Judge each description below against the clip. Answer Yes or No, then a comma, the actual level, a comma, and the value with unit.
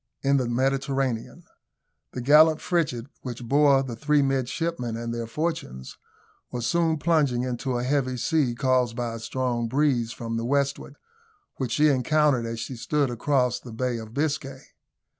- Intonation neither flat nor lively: Yes, average, 3.4 semitones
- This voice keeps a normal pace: Yes, average, 160 wpm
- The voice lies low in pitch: Yes, low, 130 Hz